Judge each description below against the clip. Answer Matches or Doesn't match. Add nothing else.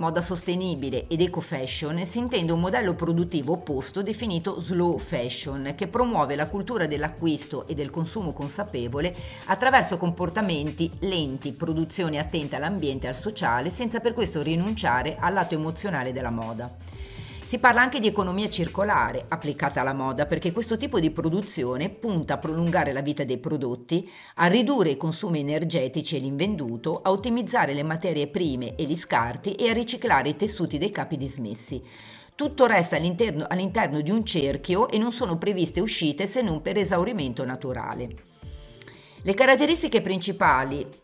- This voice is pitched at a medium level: Matches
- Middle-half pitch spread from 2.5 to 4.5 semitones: Doesn't match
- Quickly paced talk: Doesn't match